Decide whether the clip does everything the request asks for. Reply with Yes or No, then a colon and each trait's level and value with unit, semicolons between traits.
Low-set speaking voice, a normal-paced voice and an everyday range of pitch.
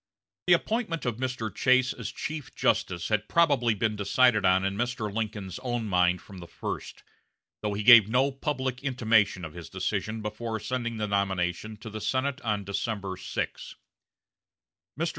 Yes: low, 110 Hz; average, 160 wpm; average, 4.2 semitones